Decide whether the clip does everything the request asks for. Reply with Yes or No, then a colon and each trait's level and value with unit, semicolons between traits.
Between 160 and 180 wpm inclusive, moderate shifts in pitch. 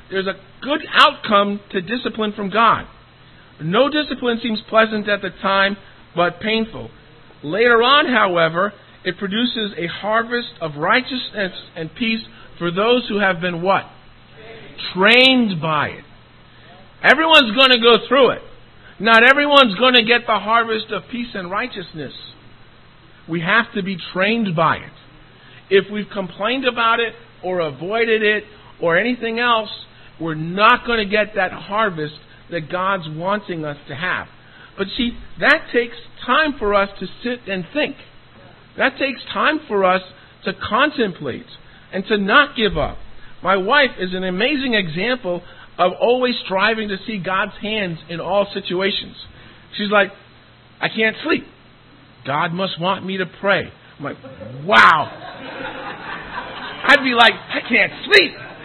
No: average, 145 wpm; average, 4.9 semitones